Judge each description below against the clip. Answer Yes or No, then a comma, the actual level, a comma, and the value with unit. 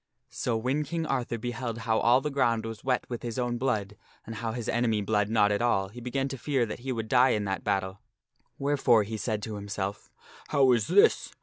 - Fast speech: Yes, fast, 220 wpm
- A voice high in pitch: No, low, 115 Hz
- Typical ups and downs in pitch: Yes, average, 3.2 semitones